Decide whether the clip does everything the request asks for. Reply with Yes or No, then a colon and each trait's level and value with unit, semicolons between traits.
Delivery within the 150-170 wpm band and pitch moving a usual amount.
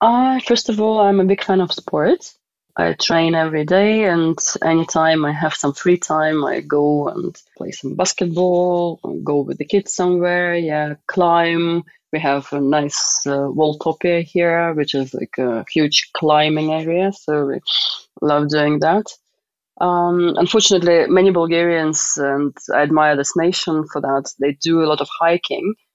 Yes: average, 165 wpm; average, 3.0 semitones